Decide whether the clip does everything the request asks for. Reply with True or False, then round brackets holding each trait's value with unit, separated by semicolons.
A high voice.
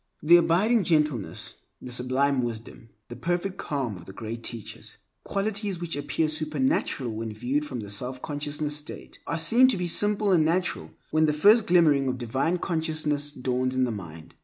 False (150 Hz)